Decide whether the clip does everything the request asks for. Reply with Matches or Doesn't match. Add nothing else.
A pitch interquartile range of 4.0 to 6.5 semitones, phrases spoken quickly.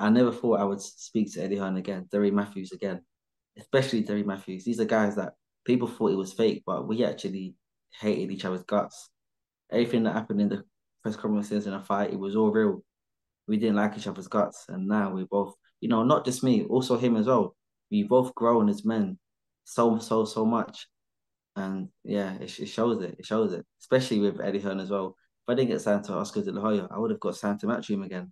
Doesn't match